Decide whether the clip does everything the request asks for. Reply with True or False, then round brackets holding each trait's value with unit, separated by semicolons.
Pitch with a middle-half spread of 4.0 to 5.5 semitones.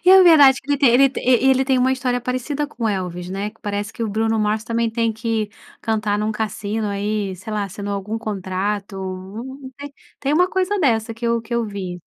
False (3.6 semitones)